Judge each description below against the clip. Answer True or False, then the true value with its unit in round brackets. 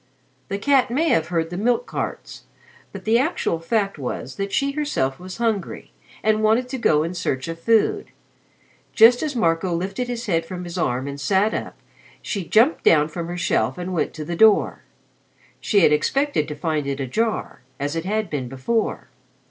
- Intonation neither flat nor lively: False (6.2 semitones)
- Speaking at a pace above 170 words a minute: True (190 wpm)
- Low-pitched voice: False (185 Hz)